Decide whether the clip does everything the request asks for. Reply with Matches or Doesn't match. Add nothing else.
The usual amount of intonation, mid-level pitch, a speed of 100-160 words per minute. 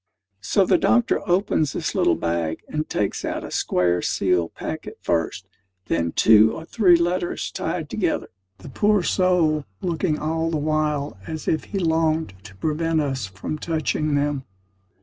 Doesn't match